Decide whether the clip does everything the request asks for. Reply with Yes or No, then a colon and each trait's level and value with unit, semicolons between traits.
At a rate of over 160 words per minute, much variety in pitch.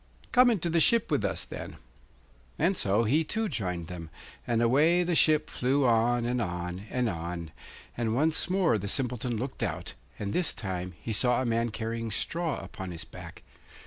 Yes: average, 180 wpm; wide, 7.4 semitones